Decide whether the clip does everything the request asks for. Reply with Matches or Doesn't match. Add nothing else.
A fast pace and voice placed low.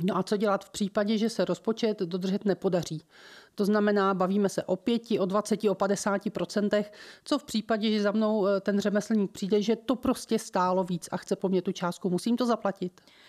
Doesn't match